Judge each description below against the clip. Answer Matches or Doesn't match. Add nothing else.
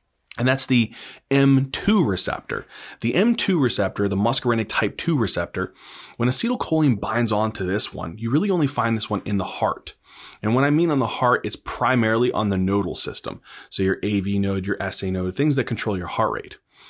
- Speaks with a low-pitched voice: Matches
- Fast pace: Doesn't match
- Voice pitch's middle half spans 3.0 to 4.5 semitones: Doesn't match